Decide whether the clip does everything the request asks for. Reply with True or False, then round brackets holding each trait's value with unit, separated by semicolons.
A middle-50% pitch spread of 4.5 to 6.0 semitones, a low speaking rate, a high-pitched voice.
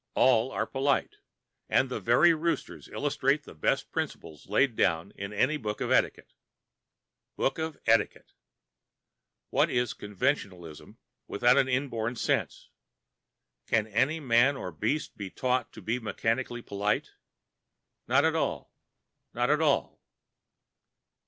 False (4.8 semitones; 125 wpm; 120 Hz)